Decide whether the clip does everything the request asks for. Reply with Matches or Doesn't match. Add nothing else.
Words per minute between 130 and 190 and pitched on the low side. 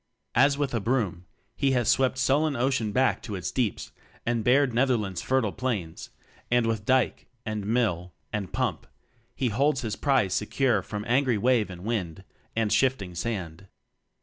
Matches